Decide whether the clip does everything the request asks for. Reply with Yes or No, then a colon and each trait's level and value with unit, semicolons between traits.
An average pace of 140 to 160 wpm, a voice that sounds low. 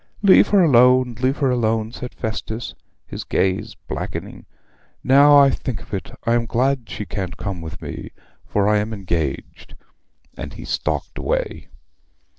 Yes: average, 155 wpm; low, 115 Hz